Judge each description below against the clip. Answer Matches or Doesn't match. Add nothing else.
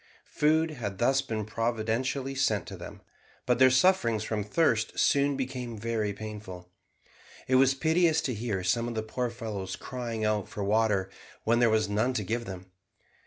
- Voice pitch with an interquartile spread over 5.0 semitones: Doesn't match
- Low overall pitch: Matches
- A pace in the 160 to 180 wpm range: Matches